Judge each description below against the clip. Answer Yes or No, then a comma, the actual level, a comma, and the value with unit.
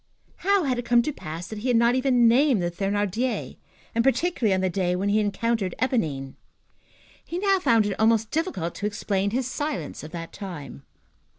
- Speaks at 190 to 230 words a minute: Yes, average, 195 wpm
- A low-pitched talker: No, high, 220 Hz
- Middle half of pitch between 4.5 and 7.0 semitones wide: Yes, wide, 5.4 semitones